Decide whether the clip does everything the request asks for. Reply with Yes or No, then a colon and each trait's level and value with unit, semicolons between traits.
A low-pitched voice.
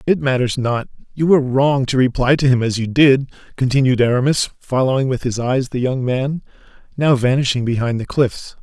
Yes: low, 130 Hz